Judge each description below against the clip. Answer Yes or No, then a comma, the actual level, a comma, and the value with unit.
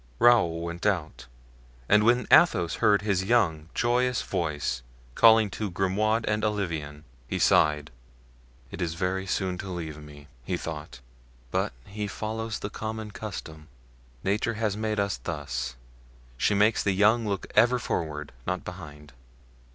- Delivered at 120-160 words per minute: Yes, average, 145 wpm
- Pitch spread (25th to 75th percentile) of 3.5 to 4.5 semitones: No, wide, 5.4 semitones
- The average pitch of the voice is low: Yes, low, 100 Hz